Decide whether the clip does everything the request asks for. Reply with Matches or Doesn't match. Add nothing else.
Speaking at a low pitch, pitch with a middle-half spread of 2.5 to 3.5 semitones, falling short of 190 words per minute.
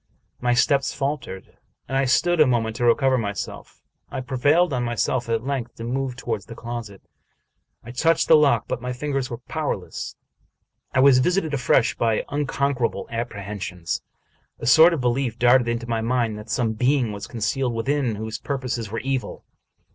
Matches